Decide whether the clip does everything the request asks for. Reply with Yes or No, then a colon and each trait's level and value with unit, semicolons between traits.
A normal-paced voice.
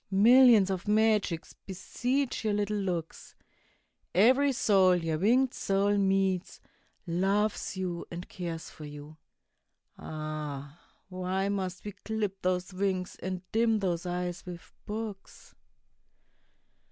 No: slow, 115 wpm